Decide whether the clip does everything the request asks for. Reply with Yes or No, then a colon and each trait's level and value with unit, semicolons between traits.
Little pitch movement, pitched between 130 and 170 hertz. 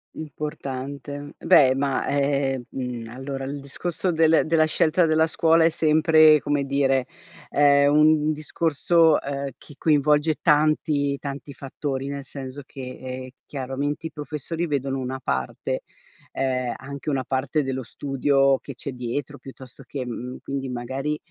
Yes: narrow, 2.3 semitones; medium, 140 Hz